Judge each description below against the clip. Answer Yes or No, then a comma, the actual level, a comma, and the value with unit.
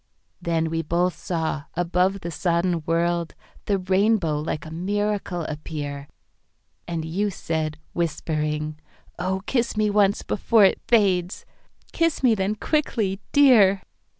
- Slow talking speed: Yes, slow, 110 wpm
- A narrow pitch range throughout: No, average, 4.0 semitones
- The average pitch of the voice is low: No, medium, 175 Hz